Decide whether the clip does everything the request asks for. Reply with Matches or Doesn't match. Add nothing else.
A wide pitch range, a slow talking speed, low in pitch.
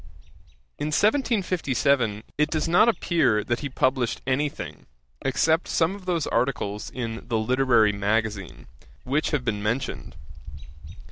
Matches